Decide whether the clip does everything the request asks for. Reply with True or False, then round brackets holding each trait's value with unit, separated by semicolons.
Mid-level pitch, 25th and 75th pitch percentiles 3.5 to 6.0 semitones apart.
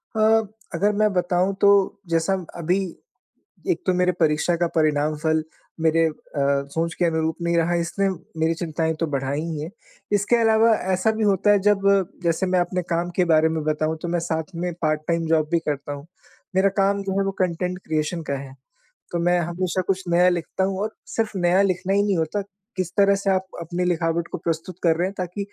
False (175 Hz; 2.9 semitones)